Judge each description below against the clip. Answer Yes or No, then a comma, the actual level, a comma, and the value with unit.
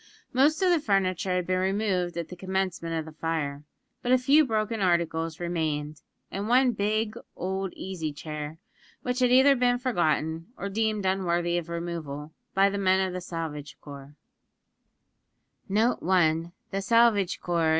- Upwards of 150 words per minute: No, average, 140 wpm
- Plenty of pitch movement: No, average, 4.7 semitones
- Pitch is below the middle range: No, medium, 185 Hz